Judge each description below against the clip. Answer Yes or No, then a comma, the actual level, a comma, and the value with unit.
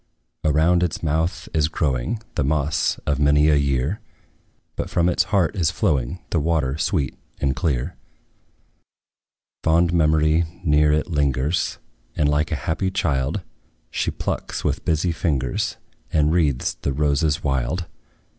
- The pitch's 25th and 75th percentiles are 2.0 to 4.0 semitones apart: Yes, average, 2.9 semitones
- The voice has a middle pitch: No, very low, 75 Hz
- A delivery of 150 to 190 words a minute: No, slow, 135 wpm